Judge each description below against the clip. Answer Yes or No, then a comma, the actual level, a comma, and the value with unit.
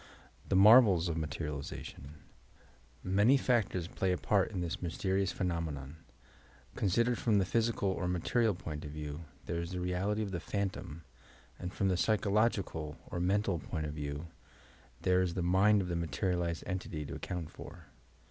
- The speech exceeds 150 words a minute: Yes, average, 165 wpm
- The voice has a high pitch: No, very low, 90 Hz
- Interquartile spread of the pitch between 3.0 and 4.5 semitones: Yes, average, 3.3 semitones